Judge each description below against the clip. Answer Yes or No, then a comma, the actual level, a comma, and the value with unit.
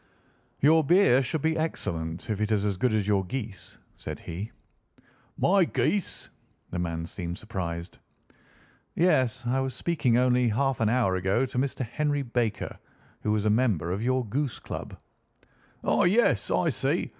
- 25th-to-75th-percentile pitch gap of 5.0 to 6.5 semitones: Yes, wide, 5.4 semitones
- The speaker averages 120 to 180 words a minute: Yes, average, 160 wpm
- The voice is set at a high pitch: No, low, 120 Hz